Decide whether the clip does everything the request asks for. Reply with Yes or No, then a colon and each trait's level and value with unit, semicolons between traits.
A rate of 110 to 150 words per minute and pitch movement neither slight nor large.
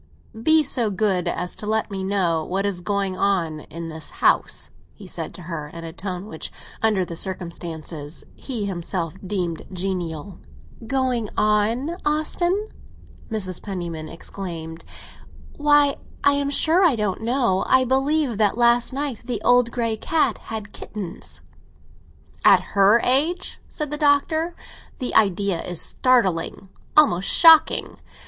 No: average, 140 wpm; wide, 6.6 semitones